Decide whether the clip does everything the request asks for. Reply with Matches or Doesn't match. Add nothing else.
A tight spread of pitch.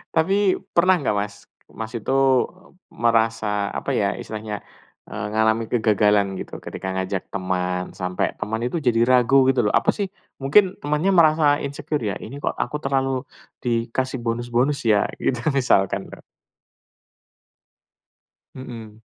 Doesn't match